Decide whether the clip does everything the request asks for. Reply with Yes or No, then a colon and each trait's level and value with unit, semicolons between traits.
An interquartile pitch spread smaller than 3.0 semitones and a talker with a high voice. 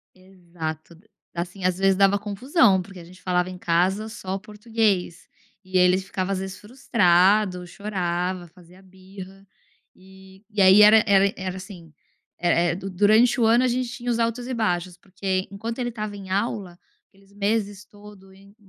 Yes: narrow, 2.4 semitones; high, 195 Hz